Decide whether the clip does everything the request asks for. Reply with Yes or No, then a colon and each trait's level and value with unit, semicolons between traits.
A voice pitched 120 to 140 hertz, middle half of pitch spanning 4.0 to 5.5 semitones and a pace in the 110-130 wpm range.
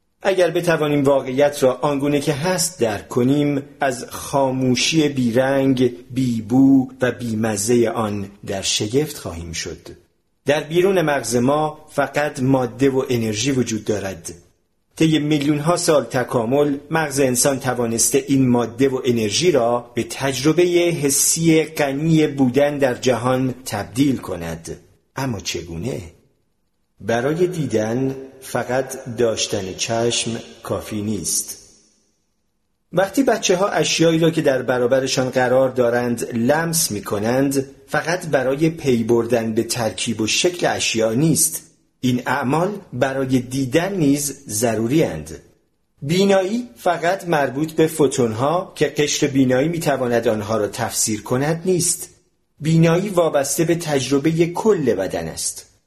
Yes: low, 135 Hz; average, 4.3 semitones; average, 120 wpm